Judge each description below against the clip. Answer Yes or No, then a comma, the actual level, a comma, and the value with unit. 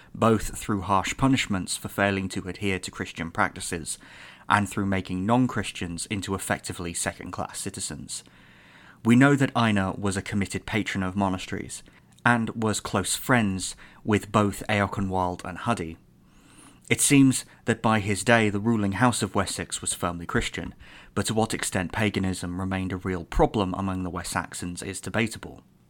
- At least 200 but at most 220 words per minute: No, average, 155 wpm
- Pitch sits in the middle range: No, low, 100 Hz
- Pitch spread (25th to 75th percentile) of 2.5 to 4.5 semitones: Yes, average, 2.8 semitones